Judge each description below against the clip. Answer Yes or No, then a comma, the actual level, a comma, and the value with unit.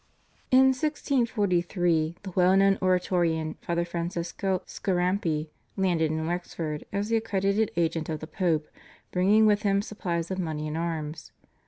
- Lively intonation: No, average, 3.4 semitones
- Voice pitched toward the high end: No, medium, 180 Hz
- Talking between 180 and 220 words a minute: No, average, 140 wpm